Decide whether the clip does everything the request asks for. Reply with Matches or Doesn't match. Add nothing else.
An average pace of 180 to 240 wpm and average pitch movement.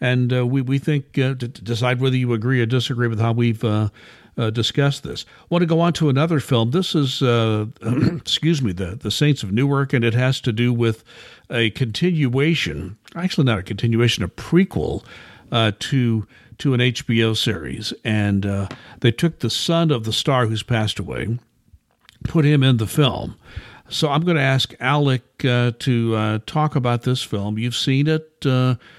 Matches